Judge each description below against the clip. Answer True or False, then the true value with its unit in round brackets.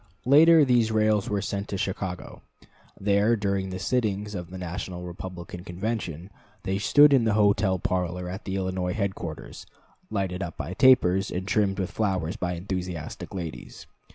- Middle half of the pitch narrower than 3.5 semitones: True (2.6 semitones)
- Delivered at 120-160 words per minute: True (155 wpm)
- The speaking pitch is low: True (95 Hz)